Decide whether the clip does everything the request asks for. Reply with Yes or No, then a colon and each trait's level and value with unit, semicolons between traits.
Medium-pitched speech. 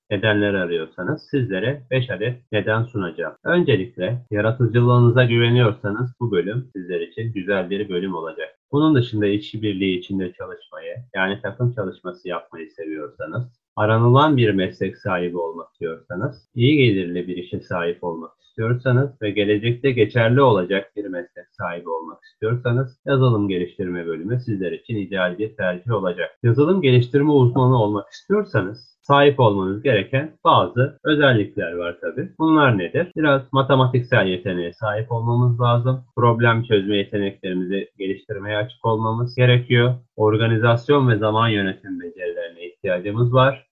No: low, 115 Hz